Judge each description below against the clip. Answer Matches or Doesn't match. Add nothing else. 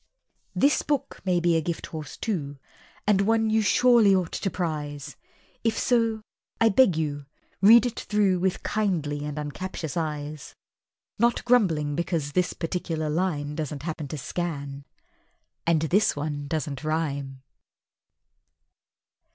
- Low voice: Doesn't match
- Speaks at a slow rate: Matches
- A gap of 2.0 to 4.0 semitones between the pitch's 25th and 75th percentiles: Doesn't match